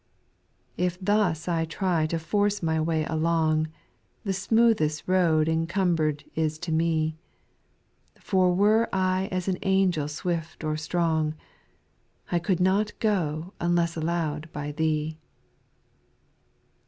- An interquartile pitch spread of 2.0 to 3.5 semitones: Yes, average, 2.9 semitones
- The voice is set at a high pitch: No, medium, 165 Hz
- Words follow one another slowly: Yes, slow, 120 wpm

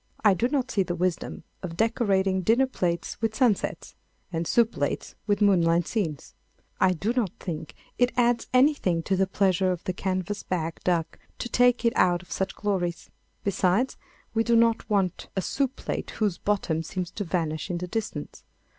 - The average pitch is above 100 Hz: Yes, high, 190 Hz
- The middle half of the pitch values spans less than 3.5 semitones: No, average, 4.5 semitones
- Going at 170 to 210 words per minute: Yes, average, 180 wpm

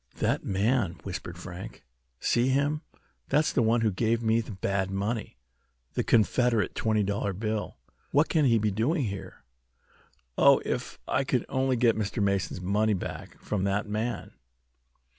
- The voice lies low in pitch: Yes, low, 110 Hz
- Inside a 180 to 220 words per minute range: No, average, 155 wpm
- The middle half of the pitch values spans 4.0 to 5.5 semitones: No, average, 3.3 semitones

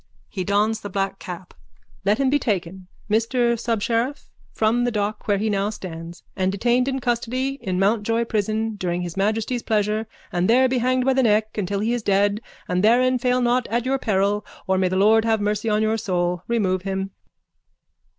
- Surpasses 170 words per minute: Yes, average, 190 wpm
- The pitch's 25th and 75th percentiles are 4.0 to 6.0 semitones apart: No, average, 3.4 semitones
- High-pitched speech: Yes, high, 215 Hz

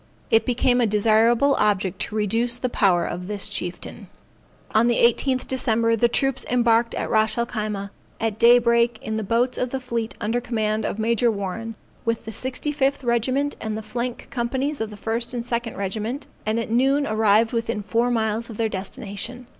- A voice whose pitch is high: Yes, high, 230 Hz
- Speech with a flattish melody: Yes, narrow, 2.1 semitones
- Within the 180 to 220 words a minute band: Yes, average, 185 wpm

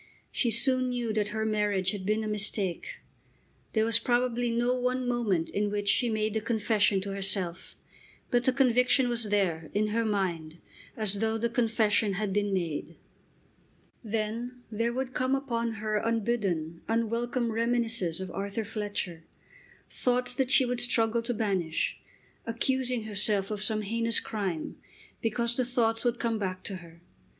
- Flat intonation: No, average, 3.0 semitones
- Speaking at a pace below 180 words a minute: Yes, average, 160 wpm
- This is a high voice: Yes, high, 220 Hz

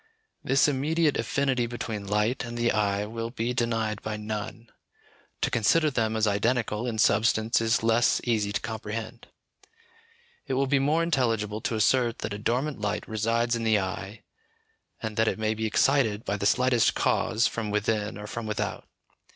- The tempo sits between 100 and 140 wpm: No, average, 170 wpm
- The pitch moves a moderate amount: No, narrow, 2.3 semitones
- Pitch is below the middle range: Yes, low, 115 Hz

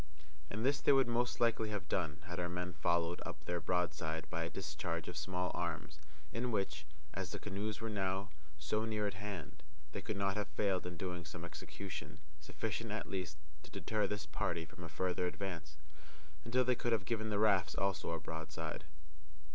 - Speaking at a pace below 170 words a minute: No, average, 190 wpm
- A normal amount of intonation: Yes, average, 3.7 semitones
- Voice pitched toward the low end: Yes, very low, 95 Hz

